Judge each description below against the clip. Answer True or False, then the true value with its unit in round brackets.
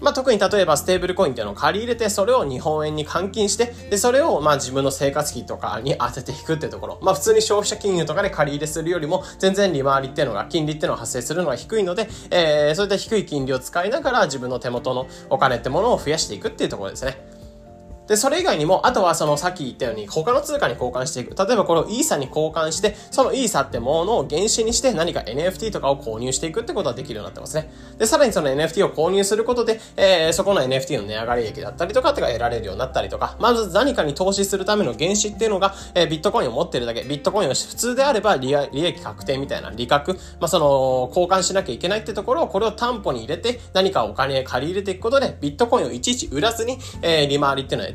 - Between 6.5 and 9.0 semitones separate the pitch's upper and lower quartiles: True (7.1 semitones)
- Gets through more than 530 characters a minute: True (540 characters per minute)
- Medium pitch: True (180 Hz)